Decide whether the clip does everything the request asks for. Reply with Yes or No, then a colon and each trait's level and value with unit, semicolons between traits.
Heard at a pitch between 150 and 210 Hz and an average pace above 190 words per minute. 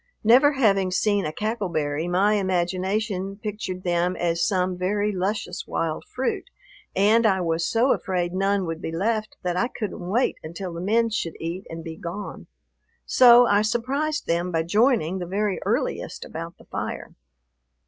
No: high, 190 Hz; average, 165 wpm